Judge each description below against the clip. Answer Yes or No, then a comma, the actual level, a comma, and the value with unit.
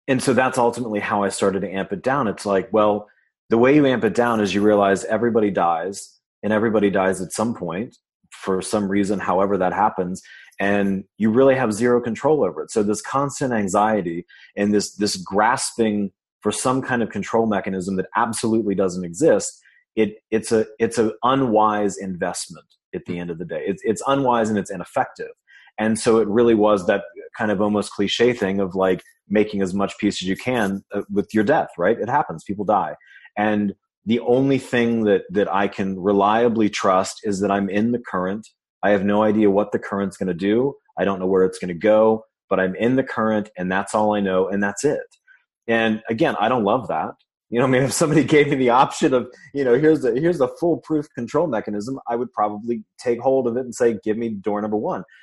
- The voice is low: Yes, low, 105 Hz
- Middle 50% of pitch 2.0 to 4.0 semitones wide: Yes, average, 3.2 semitones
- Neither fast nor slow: No, fast, 215 wpm